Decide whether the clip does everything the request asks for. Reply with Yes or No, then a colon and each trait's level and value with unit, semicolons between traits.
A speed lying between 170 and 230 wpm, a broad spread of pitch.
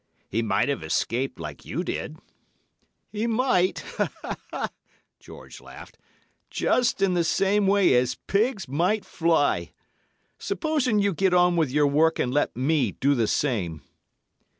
No: slow, 135 wpm; wide, 7.8 semitones